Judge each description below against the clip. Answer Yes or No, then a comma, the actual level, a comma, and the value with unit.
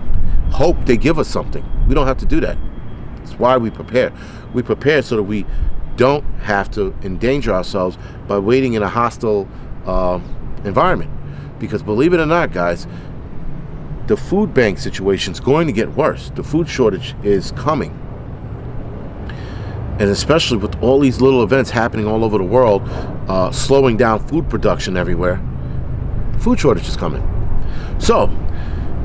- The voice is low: Yes, low, 110 Hz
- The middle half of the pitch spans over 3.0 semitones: Yes, average, 4.7 semitones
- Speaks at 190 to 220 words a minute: No, average, 155 wpm